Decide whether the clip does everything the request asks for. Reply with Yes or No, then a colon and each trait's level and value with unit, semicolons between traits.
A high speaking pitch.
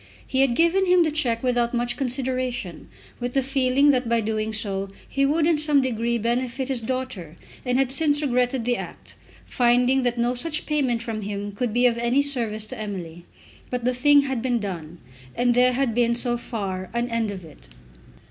Yes: high, 245 Hz